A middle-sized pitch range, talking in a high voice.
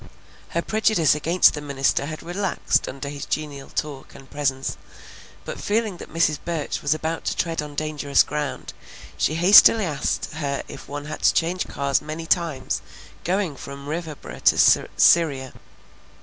No: average, 3.1 semitones; medium, 150 Hz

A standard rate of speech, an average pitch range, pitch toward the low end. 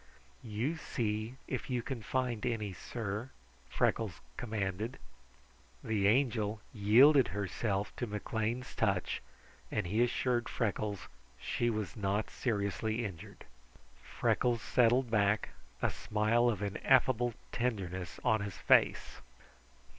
No: slow, 115 wpm; average, 3.0 semitones; low, 110 Hz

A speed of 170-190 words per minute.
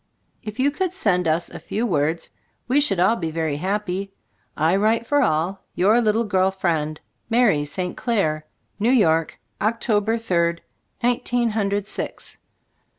No: average, 150 wpm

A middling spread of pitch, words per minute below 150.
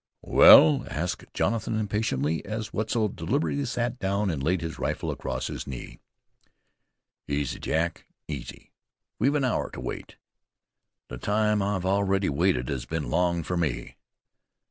No: wide, 5.8 semitones; average, 140 wpm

